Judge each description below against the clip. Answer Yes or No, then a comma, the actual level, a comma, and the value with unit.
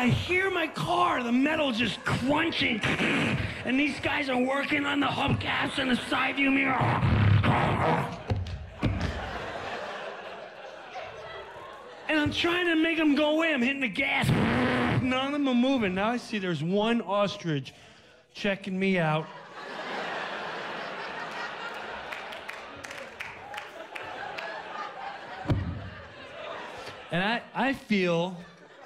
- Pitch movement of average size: No, wide, 8.8 semitones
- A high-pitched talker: Yes, high, 240 Hz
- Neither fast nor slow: No, slow, 105 wpm